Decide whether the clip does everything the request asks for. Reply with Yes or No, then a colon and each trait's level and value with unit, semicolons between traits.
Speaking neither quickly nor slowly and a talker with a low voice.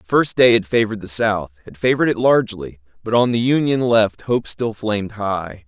No: fast, 210 wpm; low, 110 Hz